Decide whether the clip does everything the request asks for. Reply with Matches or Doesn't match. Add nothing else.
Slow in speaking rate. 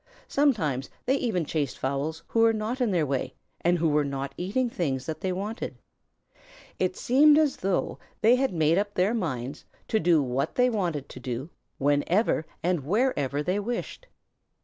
Doesn't match